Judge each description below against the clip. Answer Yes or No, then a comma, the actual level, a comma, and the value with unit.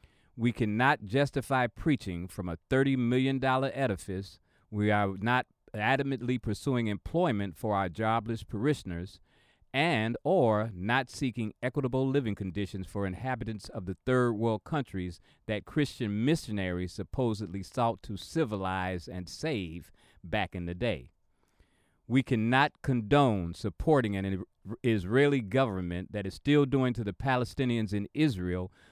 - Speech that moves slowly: Yes, slow, 130 wpm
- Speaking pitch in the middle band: No, low, 110 Hz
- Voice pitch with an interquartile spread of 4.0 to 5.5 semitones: Yes, average, 5.2 semitones